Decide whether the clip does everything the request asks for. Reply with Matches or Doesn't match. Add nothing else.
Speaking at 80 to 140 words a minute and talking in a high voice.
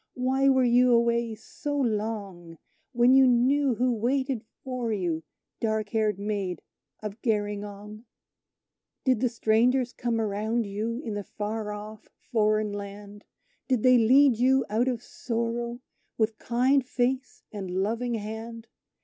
Matches